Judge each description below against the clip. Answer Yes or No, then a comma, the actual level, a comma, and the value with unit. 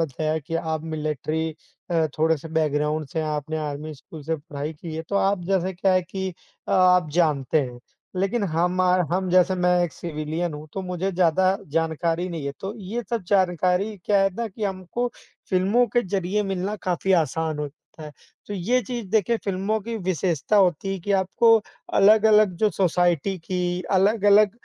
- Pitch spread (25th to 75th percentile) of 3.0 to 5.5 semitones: Yes, average, 3.5 semitones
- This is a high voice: No, medium, 180 Hz